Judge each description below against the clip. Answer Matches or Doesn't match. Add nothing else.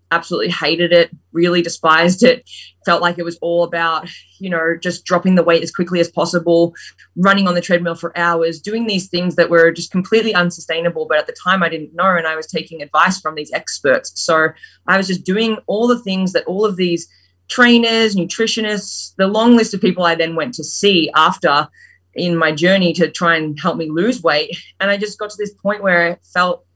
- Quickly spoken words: Matches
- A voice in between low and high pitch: Matches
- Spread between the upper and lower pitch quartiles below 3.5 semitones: Matches